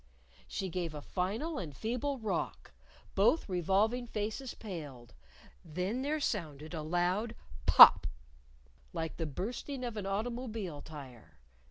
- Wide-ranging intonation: Yes, wide, 6.7 semitones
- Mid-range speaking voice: No, high, 195 Hz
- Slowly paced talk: Yes, slow, 125 wpm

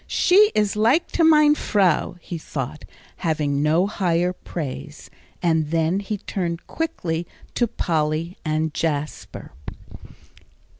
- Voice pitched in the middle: Yes, medium, 170 Hz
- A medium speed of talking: No, slow, 115 wpm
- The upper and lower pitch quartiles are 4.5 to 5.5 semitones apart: Yes, average, 4.9 semitones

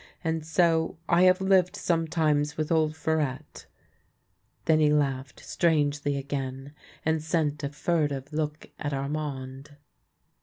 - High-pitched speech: No, medium, 150 Hz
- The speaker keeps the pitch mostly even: Yes, narrow, 2.2 semitones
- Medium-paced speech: No, slow, 120 wpm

